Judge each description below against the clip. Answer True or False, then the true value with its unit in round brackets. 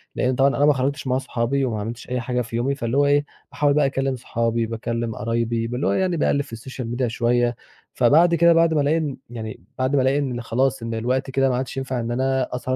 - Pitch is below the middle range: True (130 Hz)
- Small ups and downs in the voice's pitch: False (3.0 semitones)